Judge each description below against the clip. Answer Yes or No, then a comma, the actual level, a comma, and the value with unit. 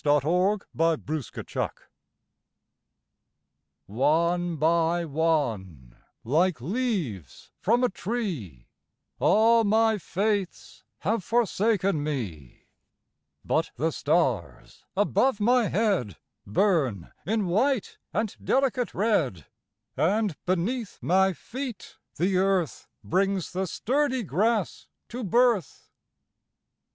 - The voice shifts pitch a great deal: Yes, wide, 6.3 semitones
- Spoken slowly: Yes, slow, 80 wpm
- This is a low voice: No, medium, 185 Hz